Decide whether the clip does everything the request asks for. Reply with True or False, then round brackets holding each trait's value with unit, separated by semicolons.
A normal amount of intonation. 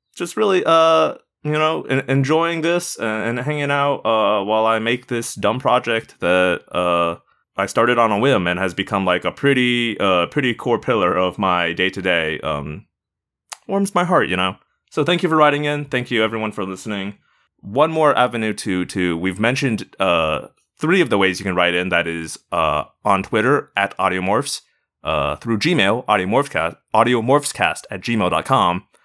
False (7.1 semitones)